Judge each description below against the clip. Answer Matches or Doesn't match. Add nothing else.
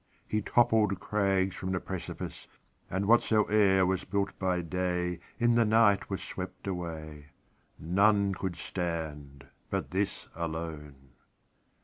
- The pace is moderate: Doesn't match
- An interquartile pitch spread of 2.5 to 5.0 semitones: Matches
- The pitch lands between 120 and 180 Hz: Doesn't match